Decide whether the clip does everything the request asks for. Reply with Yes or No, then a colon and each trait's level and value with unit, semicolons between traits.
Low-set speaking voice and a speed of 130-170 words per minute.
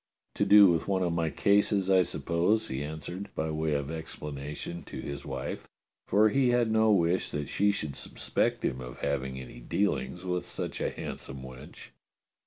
No: very low, 80 Hz; average, 180 wpm